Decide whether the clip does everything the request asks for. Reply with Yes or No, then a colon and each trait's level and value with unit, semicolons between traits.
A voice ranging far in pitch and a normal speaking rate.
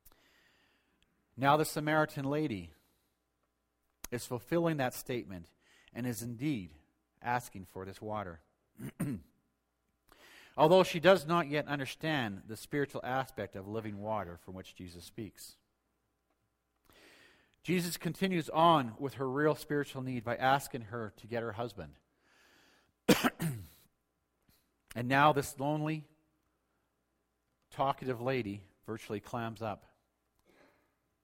No: wide, 8.7 semitones; slow, 105 wpm